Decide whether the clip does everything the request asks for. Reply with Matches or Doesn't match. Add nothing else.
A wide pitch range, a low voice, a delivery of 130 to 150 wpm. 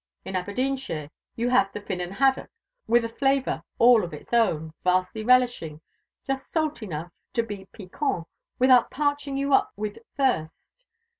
Doesn't match